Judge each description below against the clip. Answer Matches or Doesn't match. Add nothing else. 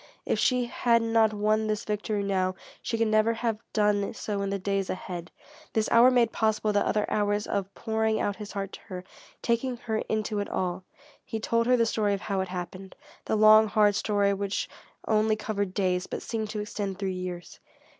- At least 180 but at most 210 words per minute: Matches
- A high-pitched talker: Matches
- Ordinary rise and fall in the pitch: Doesn't match